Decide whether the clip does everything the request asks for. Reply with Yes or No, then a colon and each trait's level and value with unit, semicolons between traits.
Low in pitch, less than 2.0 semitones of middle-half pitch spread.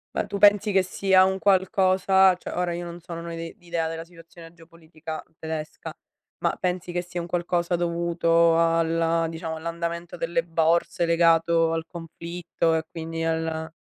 No: medium, 170 Hz; narrow, 1.2 semitones